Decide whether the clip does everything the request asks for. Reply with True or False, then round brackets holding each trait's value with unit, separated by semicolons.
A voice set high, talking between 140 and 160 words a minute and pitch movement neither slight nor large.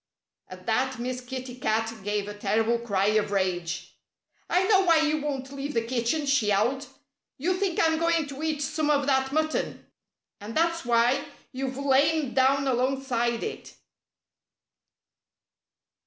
True (265 Hz; 145 wpm; 4.5 semitones)